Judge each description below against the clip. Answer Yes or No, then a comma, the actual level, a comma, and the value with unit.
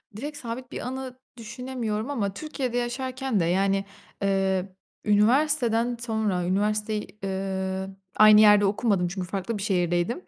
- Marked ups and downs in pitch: No, average, 4.1 semitones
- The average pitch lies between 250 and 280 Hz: No, high, 215 Hz